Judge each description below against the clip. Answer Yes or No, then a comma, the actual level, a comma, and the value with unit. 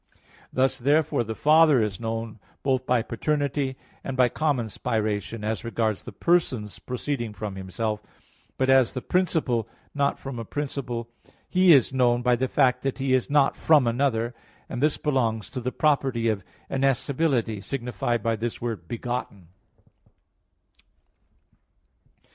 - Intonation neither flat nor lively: Yes, average, 3.5 semitones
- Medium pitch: No, low, 125 Hz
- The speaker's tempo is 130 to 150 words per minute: Yes, average, 140 wpm